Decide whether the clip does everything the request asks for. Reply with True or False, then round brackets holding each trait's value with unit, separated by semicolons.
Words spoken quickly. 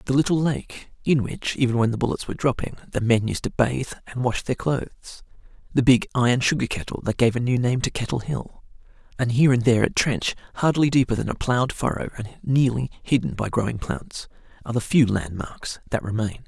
True (210 wpm)